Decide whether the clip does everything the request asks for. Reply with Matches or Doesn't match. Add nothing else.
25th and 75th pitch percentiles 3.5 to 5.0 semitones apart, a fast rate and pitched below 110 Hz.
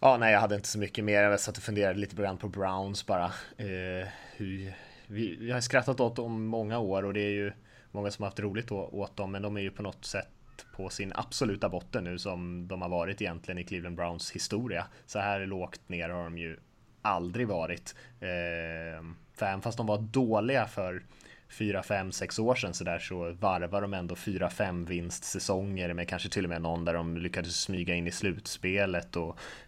Doesn't match